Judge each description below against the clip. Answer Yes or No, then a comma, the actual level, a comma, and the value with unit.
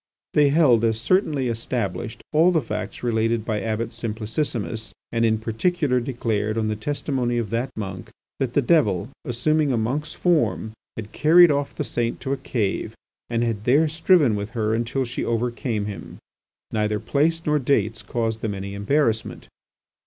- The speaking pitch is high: No, low, 115 Hz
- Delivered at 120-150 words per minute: No, average, 165 wpm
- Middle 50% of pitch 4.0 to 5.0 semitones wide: Yes, average, 4.4 semitones